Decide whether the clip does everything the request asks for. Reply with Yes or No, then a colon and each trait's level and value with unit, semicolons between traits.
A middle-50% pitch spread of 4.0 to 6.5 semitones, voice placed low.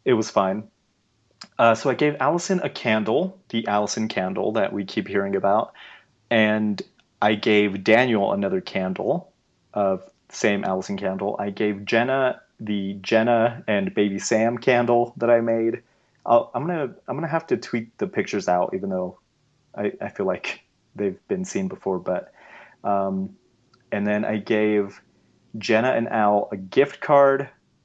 Yes: average, 4.6 semitones; low, 110 Hz